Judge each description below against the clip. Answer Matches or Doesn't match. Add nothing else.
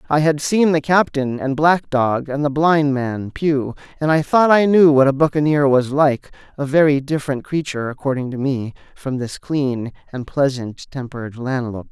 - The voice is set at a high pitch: Doesn't match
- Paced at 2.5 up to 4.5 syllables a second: Doesn't match